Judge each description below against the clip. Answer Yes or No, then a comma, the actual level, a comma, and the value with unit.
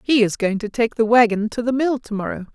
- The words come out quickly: Yes, fast, 260 wpm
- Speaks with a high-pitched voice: Yes, high, 225 Hz